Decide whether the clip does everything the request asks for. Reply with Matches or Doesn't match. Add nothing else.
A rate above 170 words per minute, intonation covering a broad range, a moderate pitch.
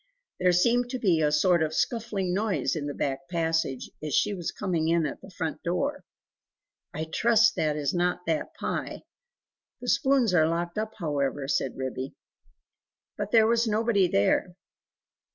Doesn't match